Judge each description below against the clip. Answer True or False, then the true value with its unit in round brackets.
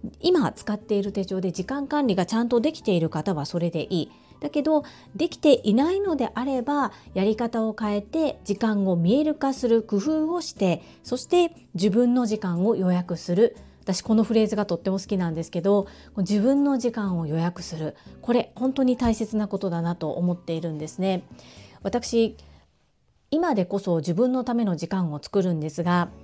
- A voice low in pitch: False (210 Hz)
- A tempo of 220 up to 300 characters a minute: False (350 characters per minute)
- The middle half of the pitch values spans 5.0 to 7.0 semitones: True (5.8 semitones)